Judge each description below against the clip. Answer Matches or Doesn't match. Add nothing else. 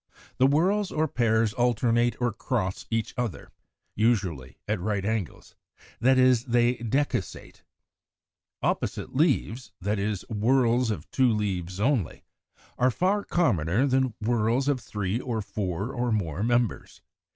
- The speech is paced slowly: Matches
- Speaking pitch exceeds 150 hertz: Doesn't match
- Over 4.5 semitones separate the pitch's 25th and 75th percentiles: Doesn't match